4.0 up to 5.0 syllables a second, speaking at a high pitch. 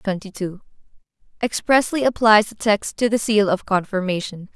Yes: 4.9 syllables/s; high, 205 Hz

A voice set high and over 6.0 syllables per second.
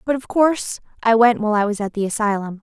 Yes: high, 225 Hz; 6.6 syllables/s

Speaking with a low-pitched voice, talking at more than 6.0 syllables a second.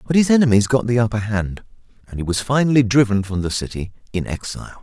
Yes: low, 115 Hz; 6.7 syllables/s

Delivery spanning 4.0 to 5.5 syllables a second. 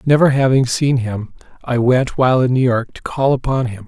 Yes: 5.2 syllables/s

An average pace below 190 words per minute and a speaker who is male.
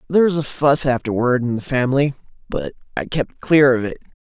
No: average, 200 wpm; male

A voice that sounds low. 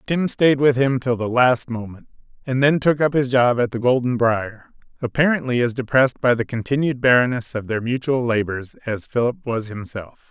Yes: low, 125 Hz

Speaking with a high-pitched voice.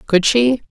Yes: high, 225 Hz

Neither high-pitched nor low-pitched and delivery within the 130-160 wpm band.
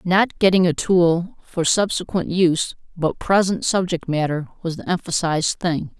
Yes: medium, 175 Hz; average, 150 wpm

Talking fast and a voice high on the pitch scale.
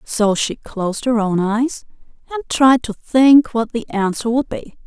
No: average, 185 wpm; high, 235 Hz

